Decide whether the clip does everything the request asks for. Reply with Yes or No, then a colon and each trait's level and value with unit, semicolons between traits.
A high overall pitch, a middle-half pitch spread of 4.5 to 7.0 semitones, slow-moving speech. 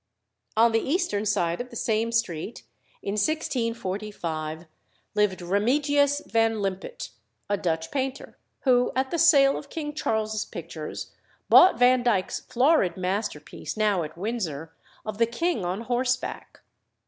Yes: high, 220 Hz; wide, 5.4 semitones; slow, 130 wpm